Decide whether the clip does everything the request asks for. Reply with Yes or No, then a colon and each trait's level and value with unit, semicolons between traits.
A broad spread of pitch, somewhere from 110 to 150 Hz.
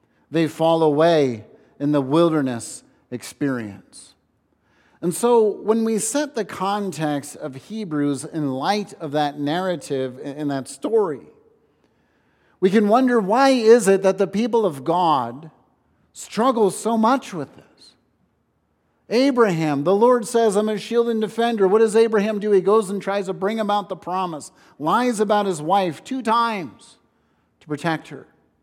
No: wide, 6.9 semitones; high, 190 Hz